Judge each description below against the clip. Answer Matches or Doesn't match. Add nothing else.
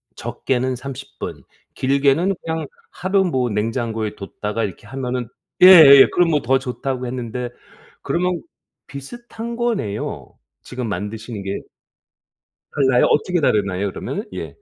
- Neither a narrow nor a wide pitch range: Doesn't match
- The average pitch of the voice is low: Matches